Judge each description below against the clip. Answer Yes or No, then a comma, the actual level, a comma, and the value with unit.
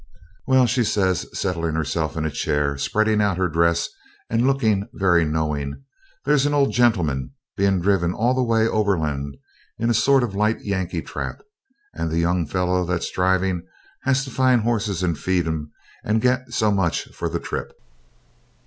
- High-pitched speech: No, very low, 95 Hz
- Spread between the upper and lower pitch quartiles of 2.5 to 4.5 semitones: No, wide, 5.5 semitones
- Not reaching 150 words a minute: No, average, 170 wpm